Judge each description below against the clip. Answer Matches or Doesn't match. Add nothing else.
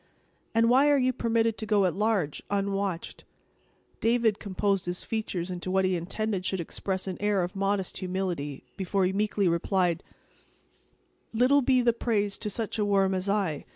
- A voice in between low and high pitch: Doesn't match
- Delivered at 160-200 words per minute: Matches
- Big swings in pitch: Doesn't match